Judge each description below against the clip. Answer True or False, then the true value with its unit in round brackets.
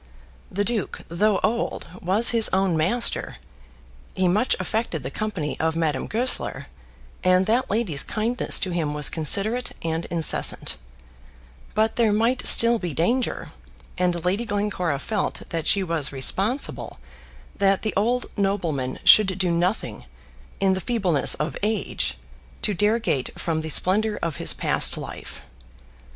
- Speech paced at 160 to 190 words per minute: False (140 wpm)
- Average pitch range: True (4.8 semitones)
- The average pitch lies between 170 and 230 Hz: True (190 Hz)